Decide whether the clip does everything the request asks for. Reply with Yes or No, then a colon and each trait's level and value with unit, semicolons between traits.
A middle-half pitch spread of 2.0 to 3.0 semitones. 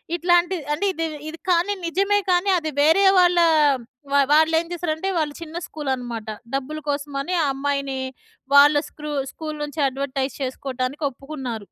No: average, 3.6 semitones